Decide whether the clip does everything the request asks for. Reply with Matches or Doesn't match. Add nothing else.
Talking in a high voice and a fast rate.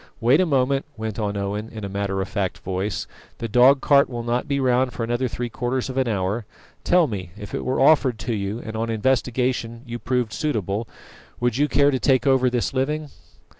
Doesn't match